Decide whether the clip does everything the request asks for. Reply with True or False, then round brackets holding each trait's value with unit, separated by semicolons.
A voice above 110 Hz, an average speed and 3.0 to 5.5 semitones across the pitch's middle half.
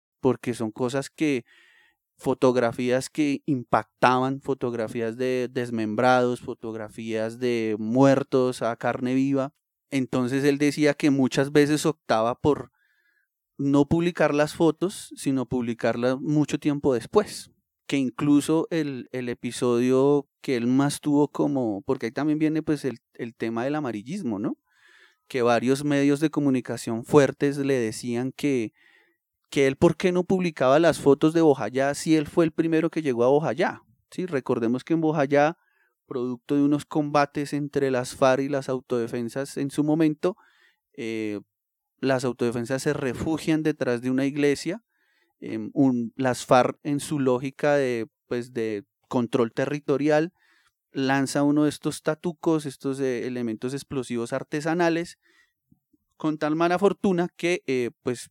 True (135 Hz; 140 wpm; 3.3 semitones)